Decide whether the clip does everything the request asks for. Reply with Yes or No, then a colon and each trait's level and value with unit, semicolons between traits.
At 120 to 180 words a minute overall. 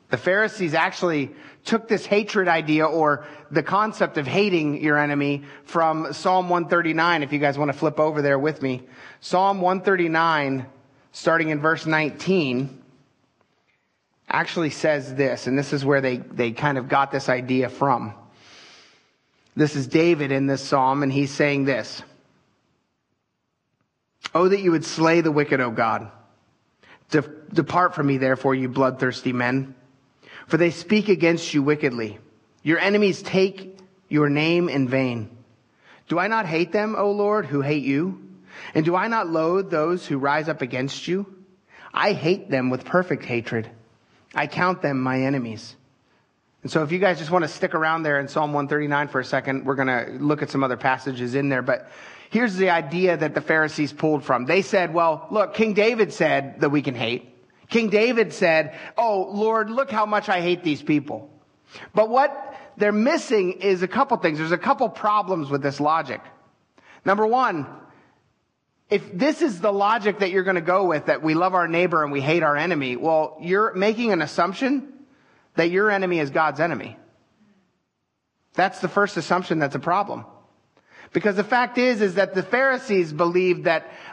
Yes: average, 175 wpm